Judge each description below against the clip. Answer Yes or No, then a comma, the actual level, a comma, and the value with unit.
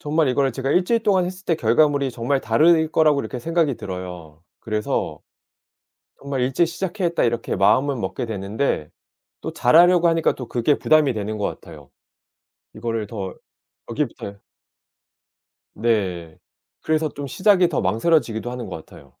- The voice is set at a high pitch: No, low, 130 Hz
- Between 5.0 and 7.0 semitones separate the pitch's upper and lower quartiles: Yes, wide, 6.7 semitones